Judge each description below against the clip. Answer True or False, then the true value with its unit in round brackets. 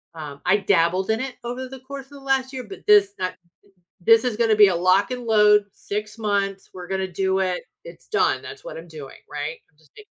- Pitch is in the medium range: False (205 Hz)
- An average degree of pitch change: True (4.7 semitones)